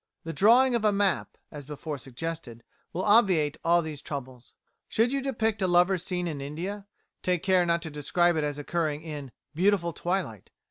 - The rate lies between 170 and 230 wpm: Yes, average, 180 wpm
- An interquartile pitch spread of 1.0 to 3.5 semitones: No, average, 4.7 semitones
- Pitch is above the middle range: No, medium, 170 Hz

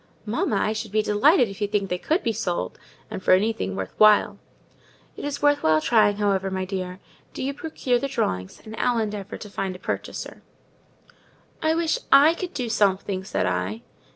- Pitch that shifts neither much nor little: Yes, average, 4.8 semitones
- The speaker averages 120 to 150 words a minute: No, average, 185 wpm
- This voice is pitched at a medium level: No, high, 210 Hz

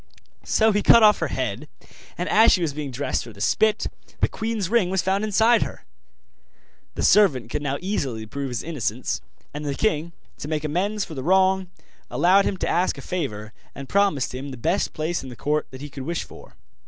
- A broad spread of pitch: Yes, wide, 6.3 semitones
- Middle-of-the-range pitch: Yes, medium, 165 Hz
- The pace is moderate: No, fast, 210 wpm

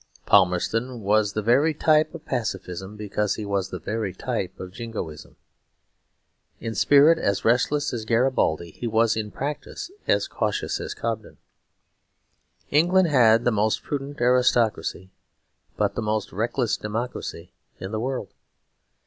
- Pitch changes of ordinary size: Yes, average, 4.3 semitones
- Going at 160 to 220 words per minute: No, slow, 135 wpm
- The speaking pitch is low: Yes, low, 115 Hz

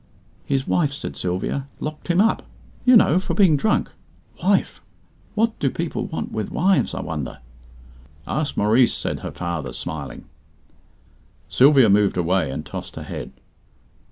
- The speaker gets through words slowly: No, average, 145 wpm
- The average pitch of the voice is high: No, low, 135 Hz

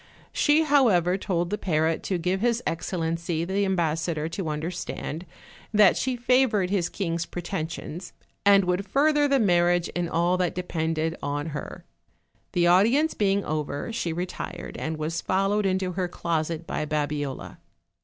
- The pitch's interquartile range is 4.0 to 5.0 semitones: No, average, 3.4 semitones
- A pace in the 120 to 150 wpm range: Yes, average, 145 wpm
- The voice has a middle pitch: Yes, medium, 175 Hz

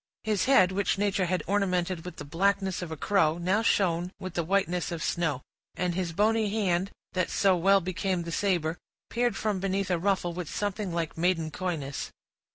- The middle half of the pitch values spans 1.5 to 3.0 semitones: Yes, narrow, 2.6 semitones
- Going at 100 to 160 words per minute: No, average, 185 wpm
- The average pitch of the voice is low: No, medium, 185 Hz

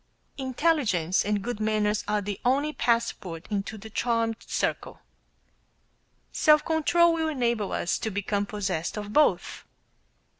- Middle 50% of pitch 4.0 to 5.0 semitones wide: Yes, average, 4.7 semitones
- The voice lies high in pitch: Yes, high, 220 Hz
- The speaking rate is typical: No, slow, 125 wpm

